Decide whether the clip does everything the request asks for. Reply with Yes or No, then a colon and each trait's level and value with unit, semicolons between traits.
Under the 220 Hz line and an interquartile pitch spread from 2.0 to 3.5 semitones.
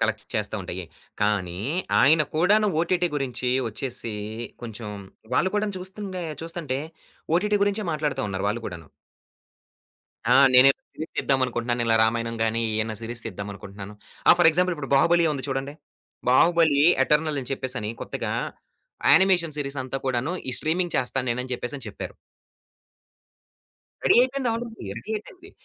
No: low, 135 Hz; wide, 6.7 semitones